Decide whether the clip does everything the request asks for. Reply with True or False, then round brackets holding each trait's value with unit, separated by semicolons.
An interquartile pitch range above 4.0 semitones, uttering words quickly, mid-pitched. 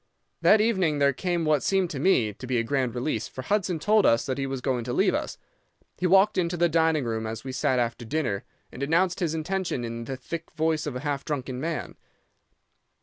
True (5.2 semitones; 220 wpm; 145 Hz)